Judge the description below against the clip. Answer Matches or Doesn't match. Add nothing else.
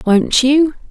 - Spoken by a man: Doesn't match